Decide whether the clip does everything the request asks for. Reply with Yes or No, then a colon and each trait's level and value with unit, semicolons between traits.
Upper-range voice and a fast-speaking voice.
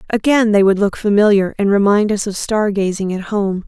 No: high, 205 Hz; average, 195 wpm